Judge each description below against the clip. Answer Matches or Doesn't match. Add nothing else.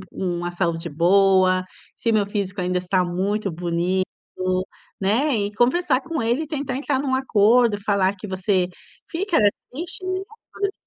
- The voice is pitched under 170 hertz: Doesn't match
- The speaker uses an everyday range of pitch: Doesn't match